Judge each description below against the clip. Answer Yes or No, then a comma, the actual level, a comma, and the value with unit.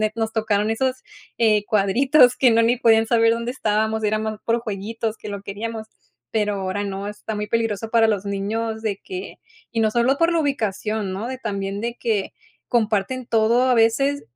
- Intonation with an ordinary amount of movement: No, narrow, 2.1 semitones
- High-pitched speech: Yes, high, 220 Hz